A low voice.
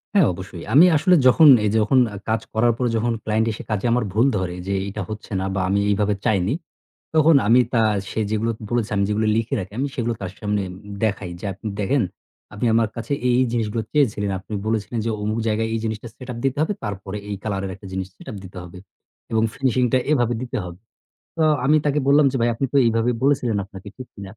Yes: low, 110 Hz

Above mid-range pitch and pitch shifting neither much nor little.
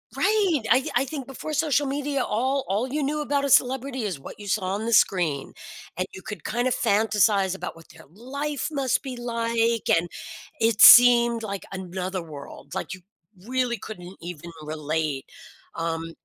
No: high, 225 Hz; wide, 6.3 semitones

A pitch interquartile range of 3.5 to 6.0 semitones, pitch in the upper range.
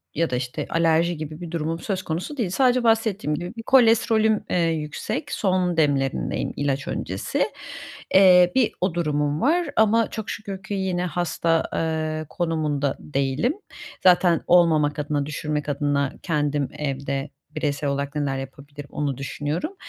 No: average, 4.3 semitones; medium, 160 Hz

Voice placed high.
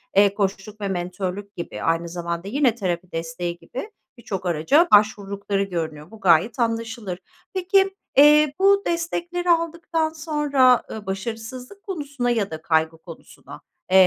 Yes: high, 210 Hz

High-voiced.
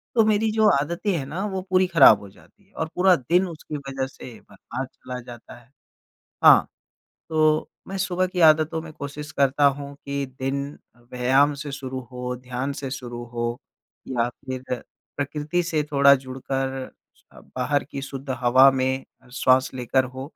No: medium, 140 Hz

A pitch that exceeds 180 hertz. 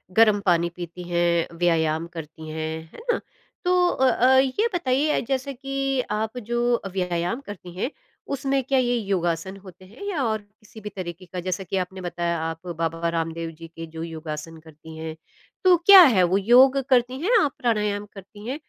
Yes: high, 190 Hz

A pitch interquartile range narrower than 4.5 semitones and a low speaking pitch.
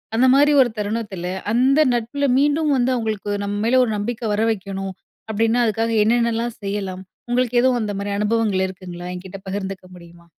No: average, 3.7 semitones; high, 220 Hz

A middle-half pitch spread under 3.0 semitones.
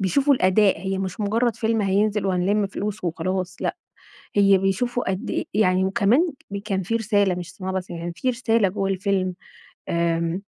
Yes: narrow, 2.4 semitones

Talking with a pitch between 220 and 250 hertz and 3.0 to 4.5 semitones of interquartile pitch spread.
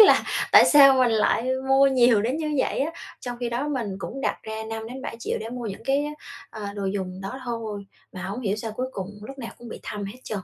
Yes: high, 235 Hz; average, 4.1 semitones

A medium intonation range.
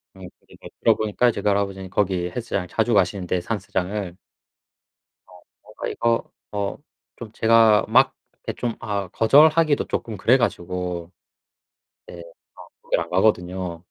Yes: average, 3.8 semitones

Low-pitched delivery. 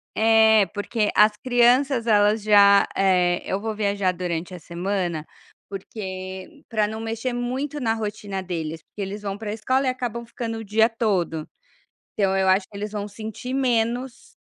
No: high, 210 Hz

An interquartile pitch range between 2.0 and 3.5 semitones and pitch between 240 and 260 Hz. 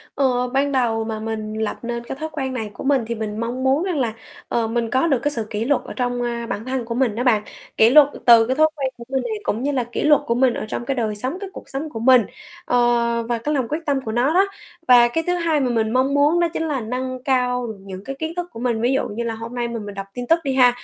Yes: average, 2.9 semitones; very high, 250 Hz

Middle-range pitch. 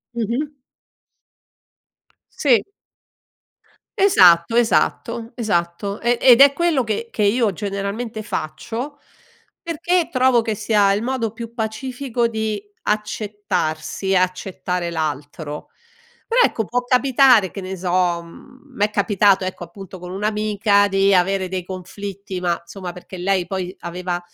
No: high, 205 Hz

